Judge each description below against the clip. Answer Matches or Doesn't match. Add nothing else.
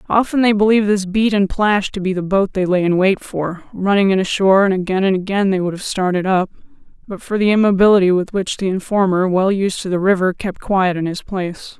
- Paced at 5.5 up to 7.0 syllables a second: Matches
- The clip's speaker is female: Matches